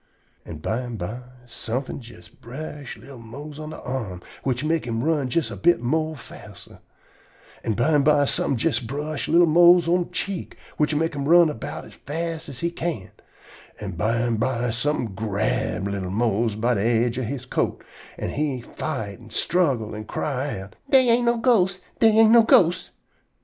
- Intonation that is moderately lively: No, wide, 6.0 semitones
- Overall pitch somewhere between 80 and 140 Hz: Yes, low, 135 Hz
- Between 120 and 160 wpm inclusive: No, average, 170 wpm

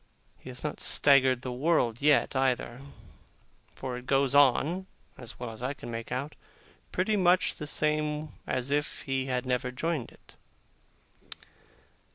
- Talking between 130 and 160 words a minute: Yes, average, 150 wpm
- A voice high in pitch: No, low, 135 Hz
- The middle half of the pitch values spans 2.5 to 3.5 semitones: Yes, average, 3.1 semitones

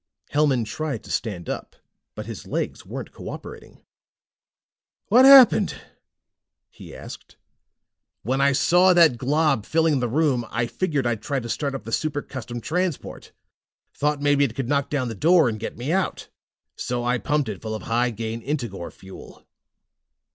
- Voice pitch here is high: No, low, 135 Hz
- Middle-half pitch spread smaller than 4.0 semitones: No, average, 4.7 semitones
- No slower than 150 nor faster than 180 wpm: Yes, average, 160 wpm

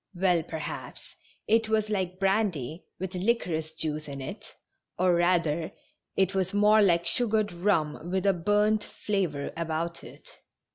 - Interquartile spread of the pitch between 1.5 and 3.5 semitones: No, average, 4.0 semitones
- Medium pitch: Yes, medium, 180 Hz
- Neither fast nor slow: Yes, average, 150 wpm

